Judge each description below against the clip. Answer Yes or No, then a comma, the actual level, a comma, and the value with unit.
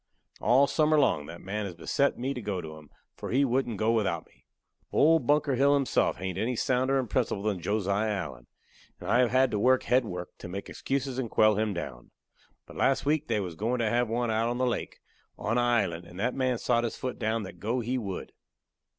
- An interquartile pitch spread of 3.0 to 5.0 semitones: Yes, average, 4.6 semitones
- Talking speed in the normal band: No, fast, 230 wpm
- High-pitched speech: No, low, 115 Hz